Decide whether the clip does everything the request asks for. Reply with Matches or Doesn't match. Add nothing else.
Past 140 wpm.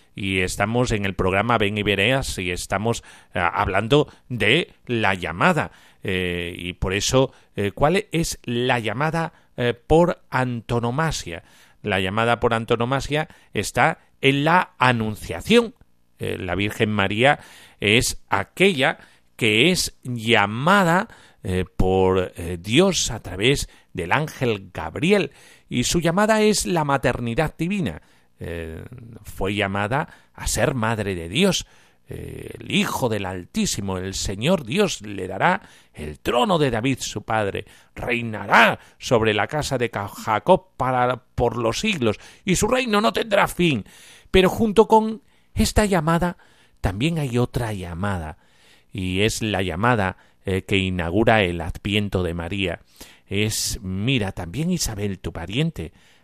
Doesn't match